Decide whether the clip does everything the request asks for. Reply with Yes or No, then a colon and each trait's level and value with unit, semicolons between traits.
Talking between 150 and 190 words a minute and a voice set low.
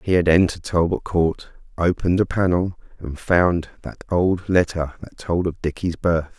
Yes: average, 170 wpm; very low, 85 Hz